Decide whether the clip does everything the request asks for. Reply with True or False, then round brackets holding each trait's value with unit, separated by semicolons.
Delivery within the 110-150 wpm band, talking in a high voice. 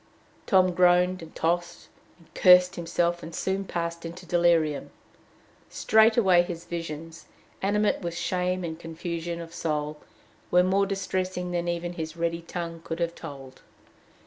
False (140 wpm; 175 Hz)